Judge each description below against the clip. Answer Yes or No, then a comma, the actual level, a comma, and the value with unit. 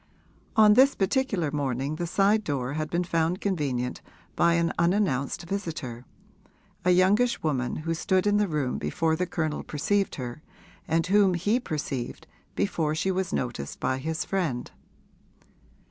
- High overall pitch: No, medium, 165 Hz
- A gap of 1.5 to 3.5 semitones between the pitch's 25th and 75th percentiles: No, average, 5.3 semitones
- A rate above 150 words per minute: No, average, 145 wpm